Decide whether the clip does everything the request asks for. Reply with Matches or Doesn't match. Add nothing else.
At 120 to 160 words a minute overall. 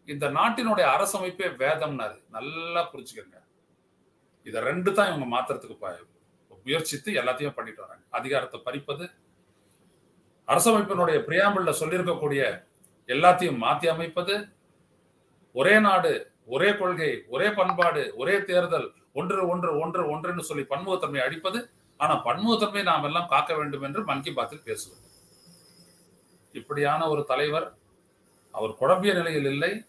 Doesn't match